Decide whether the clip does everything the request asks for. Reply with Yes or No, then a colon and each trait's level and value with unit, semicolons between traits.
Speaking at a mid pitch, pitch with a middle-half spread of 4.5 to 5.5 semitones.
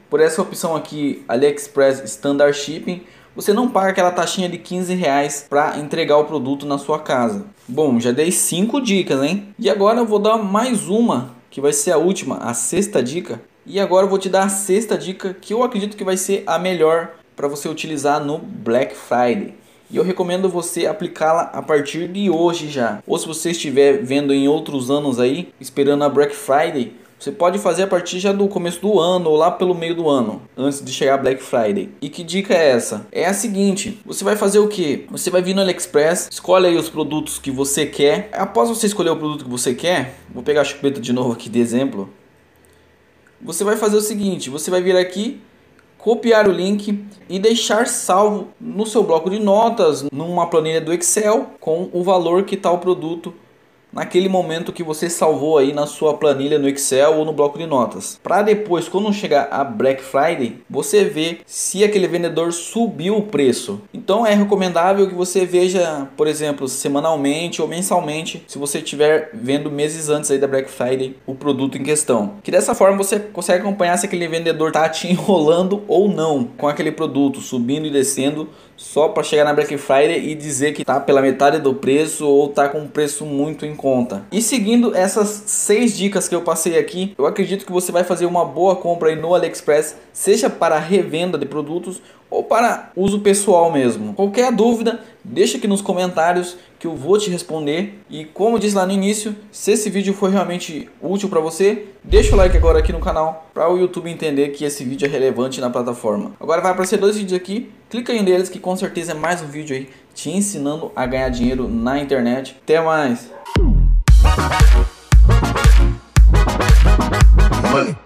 Yes: medium, 170 Hz; average, 5.1 semitones